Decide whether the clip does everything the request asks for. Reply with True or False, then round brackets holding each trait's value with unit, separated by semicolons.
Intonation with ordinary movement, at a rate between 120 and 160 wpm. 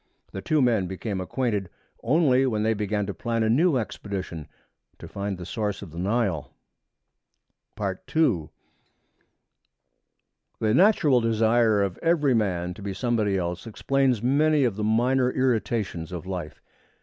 True (4.7 semitones; 140 wpm)